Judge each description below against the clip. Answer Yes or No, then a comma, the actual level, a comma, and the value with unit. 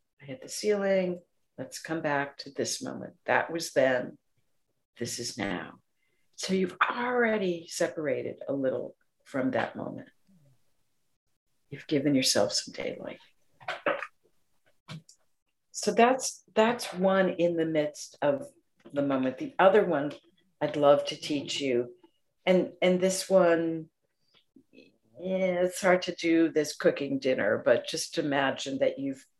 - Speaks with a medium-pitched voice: Yes, medium, 165 Hz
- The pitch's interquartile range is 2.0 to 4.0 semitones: No, average, 5.1 semitones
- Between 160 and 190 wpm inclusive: No, slow, 135 wpm